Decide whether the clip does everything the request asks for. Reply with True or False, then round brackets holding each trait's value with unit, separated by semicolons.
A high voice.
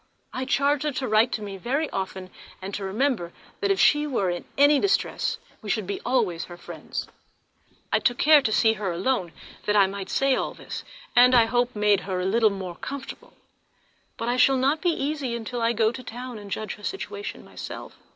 True (235 Hz)